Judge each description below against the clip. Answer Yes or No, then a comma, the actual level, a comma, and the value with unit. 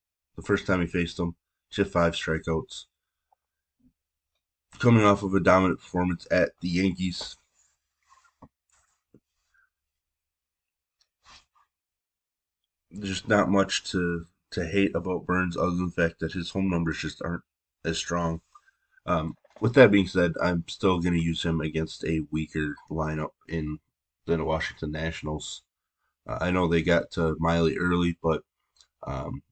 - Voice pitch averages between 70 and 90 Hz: Yes, very low, 85 Hz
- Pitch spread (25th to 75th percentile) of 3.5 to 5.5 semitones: No, average, 2.7 semitones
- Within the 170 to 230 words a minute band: No, average, 145 wpm